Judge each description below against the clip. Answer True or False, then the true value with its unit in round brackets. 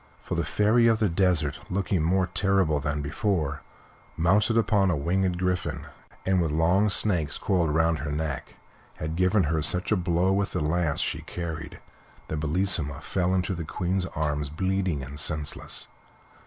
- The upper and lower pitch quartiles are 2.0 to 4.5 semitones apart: True (3.7 semitones)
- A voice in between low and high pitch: False (85 Hz)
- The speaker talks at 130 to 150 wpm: False (165 wpm)